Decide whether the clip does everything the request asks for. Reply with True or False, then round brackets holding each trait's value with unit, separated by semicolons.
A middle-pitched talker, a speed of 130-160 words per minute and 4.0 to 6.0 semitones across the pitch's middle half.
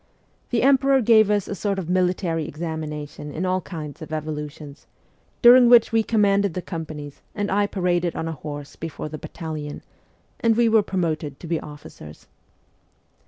False (175 Hz; 170 wpm; 5.0 semitones)